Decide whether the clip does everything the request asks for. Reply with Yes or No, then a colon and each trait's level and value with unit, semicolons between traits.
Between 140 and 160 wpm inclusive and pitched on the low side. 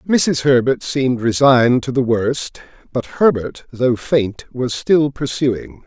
Yes: average, 145 wpm; low, 130 Hz